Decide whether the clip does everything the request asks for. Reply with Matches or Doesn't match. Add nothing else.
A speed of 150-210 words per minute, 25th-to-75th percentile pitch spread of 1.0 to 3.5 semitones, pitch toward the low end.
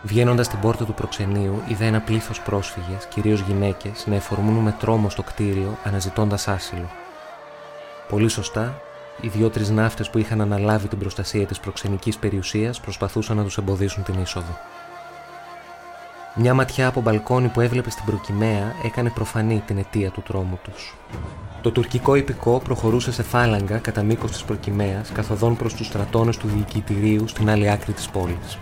Matches